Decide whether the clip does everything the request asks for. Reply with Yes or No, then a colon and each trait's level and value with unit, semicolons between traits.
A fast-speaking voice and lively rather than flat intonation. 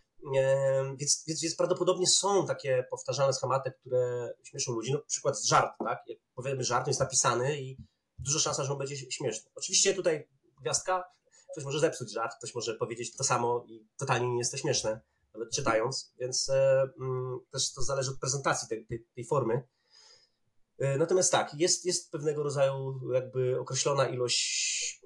Yes: fast, 170 wpm; wide, 5.7 semitones